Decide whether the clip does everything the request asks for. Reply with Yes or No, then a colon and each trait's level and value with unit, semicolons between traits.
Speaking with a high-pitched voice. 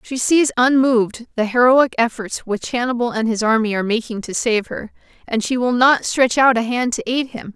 Yes: high, 240 Hz